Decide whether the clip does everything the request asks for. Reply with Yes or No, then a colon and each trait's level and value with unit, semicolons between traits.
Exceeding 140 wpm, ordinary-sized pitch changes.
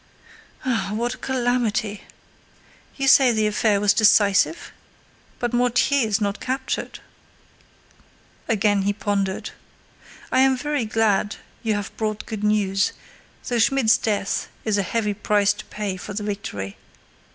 No: slow, 135 wpm; average, 3.0 semitones